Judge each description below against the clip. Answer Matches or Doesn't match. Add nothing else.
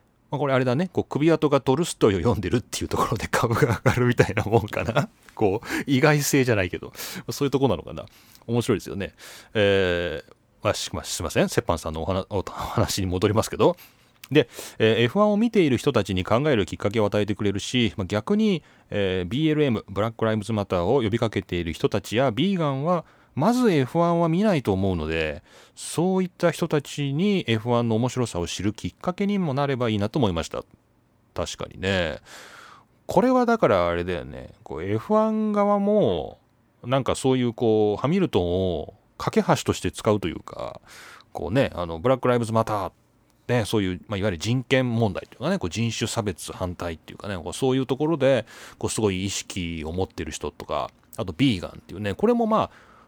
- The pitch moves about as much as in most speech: Doesn't match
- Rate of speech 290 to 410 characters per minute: Matches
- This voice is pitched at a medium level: Doesn't match